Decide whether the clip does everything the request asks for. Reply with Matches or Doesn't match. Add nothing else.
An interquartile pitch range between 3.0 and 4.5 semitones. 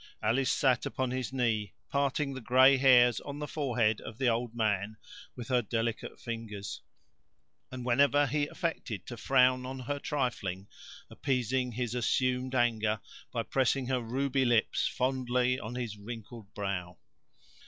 Doesn't match